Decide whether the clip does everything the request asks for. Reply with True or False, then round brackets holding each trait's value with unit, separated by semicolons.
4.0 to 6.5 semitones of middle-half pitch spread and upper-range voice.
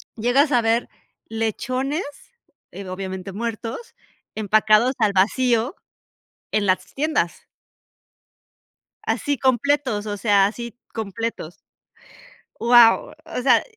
False (3.5 semitones; 225 Hz)